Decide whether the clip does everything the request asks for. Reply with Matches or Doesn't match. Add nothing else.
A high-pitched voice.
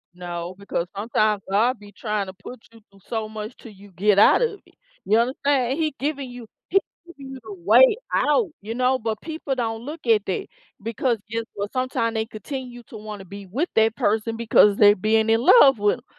Matches